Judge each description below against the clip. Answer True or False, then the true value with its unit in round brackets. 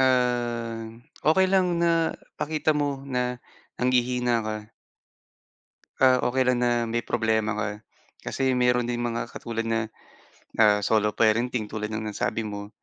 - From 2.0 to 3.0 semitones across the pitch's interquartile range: True (2.5 semitones)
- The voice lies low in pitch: True (120 Hz)